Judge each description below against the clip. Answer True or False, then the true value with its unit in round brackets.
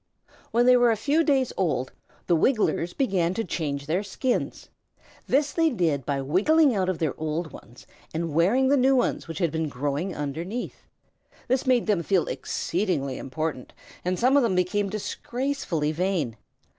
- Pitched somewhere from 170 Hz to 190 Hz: True (185 Hz)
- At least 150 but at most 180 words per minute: True (170 wpm)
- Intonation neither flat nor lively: False (7.7 semitones)